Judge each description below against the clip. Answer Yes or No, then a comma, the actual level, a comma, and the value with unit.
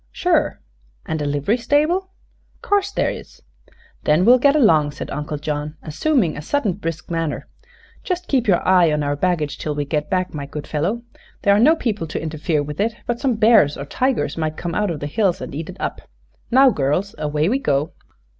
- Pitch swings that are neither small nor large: No, wide, 7.7 semitones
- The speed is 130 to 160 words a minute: No, average, 200 wpm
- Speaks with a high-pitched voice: No, medium, 170 Hz